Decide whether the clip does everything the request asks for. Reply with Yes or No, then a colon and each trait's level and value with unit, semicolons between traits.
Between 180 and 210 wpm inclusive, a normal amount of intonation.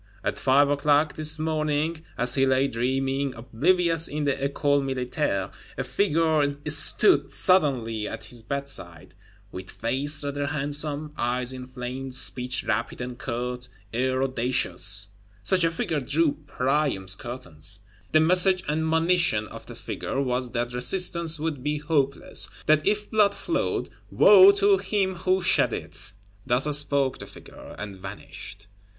No: average, 140 wpm; average, 4.2 semitones